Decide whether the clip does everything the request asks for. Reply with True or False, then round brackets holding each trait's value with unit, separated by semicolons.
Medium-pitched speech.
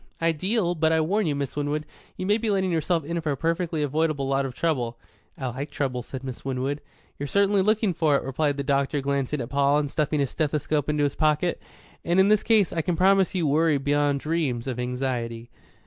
True (150 Hz)